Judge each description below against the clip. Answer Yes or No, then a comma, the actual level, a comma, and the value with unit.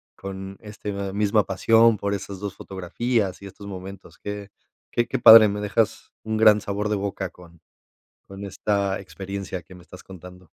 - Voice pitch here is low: Yes, low, 100 Hz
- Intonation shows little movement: Yes, narrow, 1.7 semitones